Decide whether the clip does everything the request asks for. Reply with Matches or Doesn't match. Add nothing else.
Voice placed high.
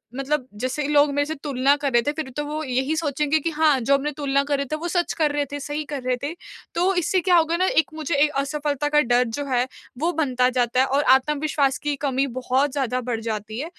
Matches